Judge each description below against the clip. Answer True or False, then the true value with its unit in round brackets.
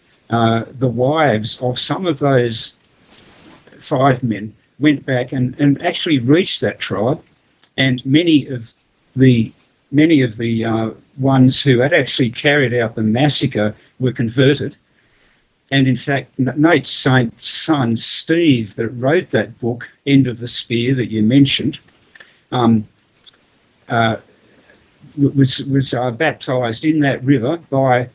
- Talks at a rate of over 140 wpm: False (135 wpm)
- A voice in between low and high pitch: False (130 Hz)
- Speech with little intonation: False (3.3 semitones)